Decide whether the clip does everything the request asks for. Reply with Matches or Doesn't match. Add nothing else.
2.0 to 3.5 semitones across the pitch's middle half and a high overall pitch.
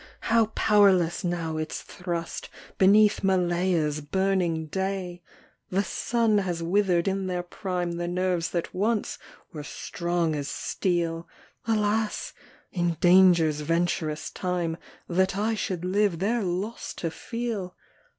Doesn't match